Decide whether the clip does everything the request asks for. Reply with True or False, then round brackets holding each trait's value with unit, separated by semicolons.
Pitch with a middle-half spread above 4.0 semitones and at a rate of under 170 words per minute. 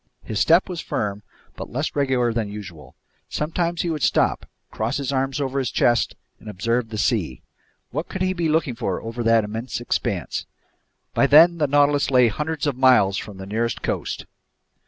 False (5.1 semitones; 180 wpm)